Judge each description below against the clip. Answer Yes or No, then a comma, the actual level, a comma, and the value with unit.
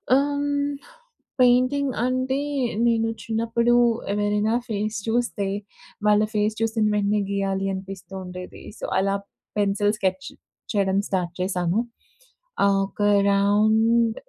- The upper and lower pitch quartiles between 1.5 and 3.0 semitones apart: Yes, average, 2.7 semitones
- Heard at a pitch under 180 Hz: No, high, 210 Hz